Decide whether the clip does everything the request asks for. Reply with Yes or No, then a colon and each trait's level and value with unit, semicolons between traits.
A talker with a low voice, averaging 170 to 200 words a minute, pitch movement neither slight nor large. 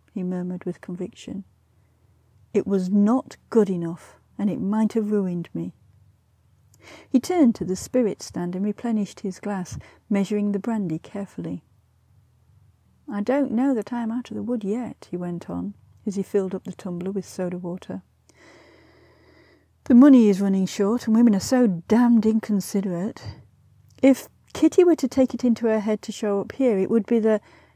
No: high, 200 Hz; average, 175 wpm; average, 4.4 semitones